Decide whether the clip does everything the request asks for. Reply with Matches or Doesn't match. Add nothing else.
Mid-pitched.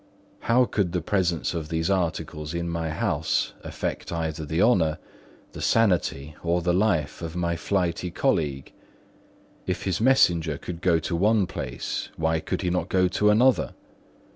Doesn't match